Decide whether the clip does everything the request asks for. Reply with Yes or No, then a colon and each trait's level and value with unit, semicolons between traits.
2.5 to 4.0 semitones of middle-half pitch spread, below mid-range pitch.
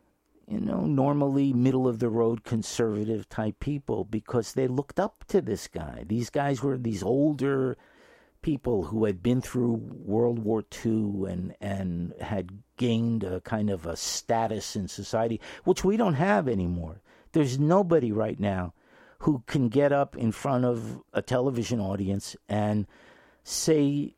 No: average, 4.8 semitones; low, 115 Hz